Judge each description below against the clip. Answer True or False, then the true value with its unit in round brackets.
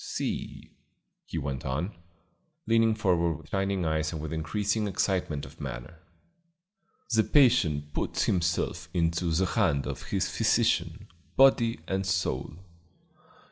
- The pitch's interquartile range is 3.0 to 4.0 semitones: False (4.5 semitones)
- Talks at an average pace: False (125 wpm)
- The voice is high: False (85 Hz)